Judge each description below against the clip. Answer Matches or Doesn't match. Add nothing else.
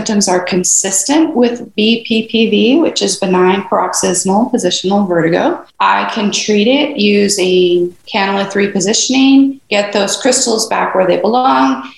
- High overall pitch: Matches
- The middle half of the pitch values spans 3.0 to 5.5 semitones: Matches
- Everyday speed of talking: Doesn't match